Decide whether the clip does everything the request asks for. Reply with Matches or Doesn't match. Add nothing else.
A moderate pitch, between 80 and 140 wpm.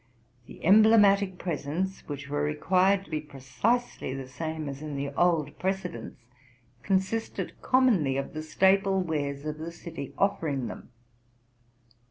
Matches